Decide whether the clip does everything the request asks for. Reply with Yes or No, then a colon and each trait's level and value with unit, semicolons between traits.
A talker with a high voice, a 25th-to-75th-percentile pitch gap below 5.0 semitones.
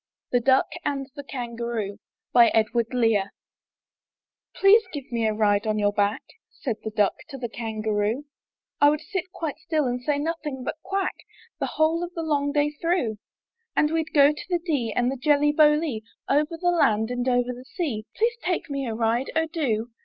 No: very high, 270 Hz; wide, 5.4 semitones